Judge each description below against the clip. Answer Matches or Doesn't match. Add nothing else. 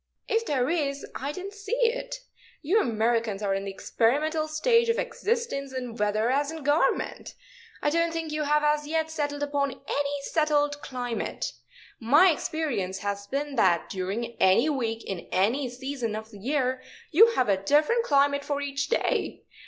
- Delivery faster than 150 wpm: Matches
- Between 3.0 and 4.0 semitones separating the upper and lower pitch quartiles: Doesn't match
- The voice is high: Matches